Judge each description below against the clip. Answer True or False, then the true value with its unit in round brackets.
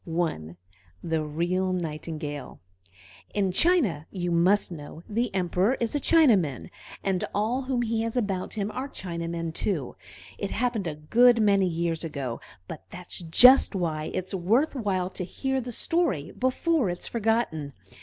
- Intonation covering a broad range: True (6.0 semitones)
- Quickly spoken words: False (155 wpm)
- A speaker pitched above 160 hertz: True (185 Hz)